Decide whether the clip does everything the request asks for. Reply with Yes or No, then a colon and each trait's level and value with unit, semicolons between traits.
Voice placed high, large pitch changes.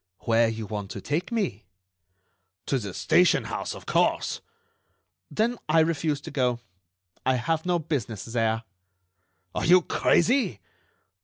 No: medium, 145 Hz; wide, 7.2 semitones